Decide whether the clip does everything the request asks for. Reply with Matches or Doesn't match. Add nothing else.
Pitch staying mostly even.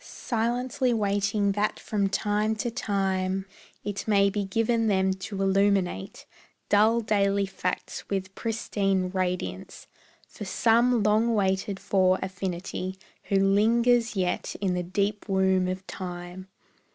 Matches